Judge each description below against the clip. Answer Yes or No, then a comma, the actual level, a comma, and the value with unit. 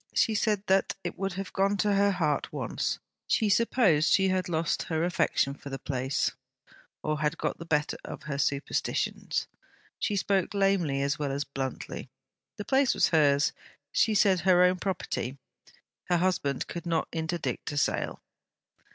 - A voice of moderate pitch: Yes, medium, 175 Hz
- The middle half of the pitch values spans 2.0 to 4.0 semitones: No, average, 4.8 semitones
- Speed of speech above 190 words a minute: No, average, 165 wpm